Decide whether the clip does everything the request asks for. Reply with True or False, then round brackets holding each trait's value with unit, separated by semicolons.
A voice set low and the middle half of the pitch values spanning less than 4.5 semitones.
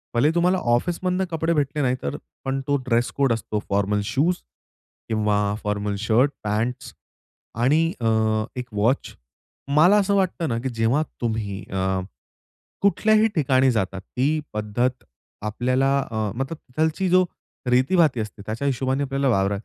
False (130 Hz; 6.0 semitones)